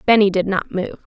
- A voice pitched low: No, high, 195 Hz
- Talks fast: Yes, fast, 210 wpm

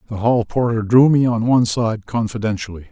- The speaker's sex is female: No, male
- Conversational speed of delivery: Yes, average, 185 wpm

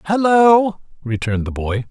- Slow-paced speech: Yes, slow, 125 wpm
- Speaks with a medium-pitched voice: Yes, medium, 160 Hz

